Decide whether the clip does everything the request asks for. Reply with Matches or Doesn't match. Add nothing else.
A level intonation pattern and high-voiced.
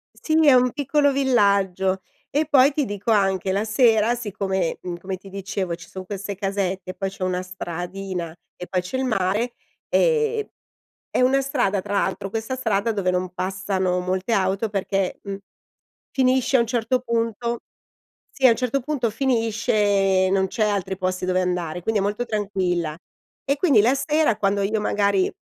Doesn't match